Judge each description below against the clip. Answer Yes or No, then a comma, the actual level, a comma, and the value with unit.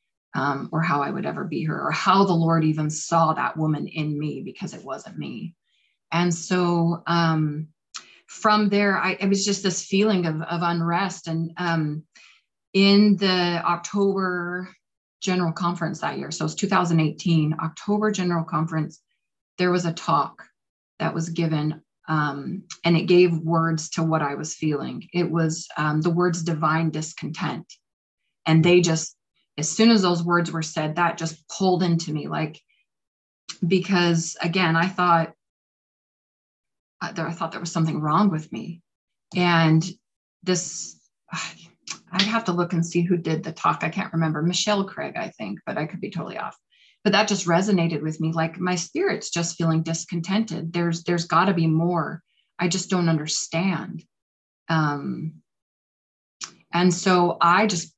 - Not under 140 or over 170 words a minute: Yes, average, 165 wpm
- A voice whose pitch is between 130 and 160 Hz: No, medium, 170 Hz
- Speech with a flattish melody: Yes, narrow, 2.0 semitones